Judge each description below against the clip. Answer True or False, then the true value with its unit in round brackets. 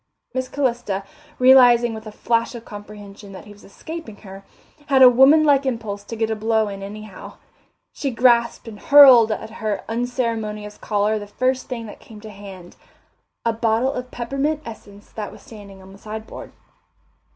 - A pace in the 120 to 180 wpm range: True (175 wpm)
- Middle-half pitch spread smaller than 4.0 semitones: True (3.3 semitones)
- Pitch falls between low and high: False (225 Hz)